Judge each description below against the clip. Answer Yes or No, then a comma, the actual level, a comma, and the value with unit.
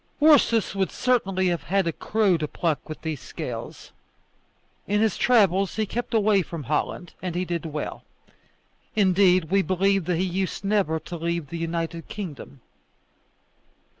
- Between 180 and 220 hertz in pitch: Yes, medium, 185 Hz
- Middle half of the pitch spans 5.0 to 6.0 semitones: No, average, 3.1 semitones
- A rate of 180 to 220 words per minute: No, average, 155 wpm